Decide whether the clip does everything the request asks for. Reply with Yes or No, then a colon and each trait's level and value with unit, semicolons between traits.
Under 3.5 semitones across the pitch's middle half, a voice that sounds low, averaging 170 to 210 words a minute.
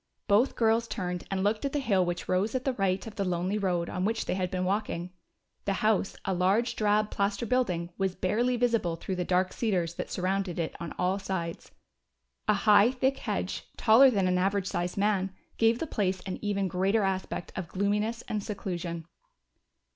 No: average, 2.9 semitones; high, 195 Hz; average, 190 wpm